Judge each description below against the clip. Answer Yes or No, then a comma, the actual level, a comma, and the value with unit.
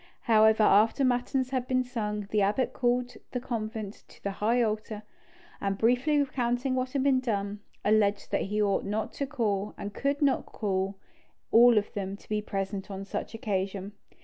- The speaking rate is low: No, average, 175 wpm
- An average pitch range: Yes, average, 3.6 semitones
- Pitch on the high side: Yes, high, 220 Hz